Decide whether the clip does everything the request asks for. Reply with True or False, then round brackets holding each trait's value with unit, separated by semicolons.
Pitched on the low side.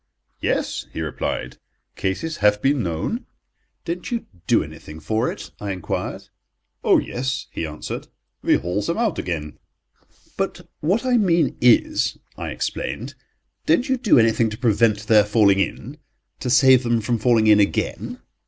True (115 Hz)